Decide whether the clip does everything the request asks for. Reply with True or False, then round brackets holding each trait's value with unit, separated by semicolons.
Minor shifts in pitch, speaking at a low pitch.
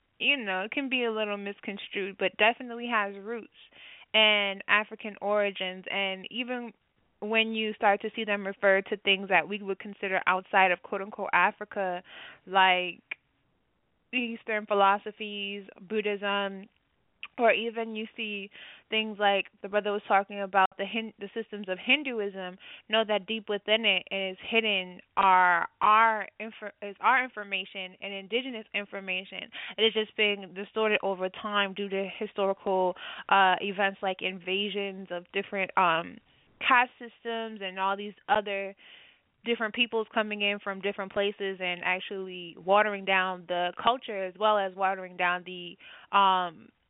False (2.1 semitones; 200 Hz)